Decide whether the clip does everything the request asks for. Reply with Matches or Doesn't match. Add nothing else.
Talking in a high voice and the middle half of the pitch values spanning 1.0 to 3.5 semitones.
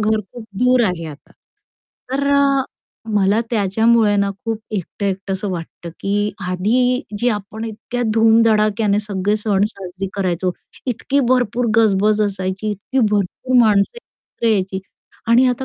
Matches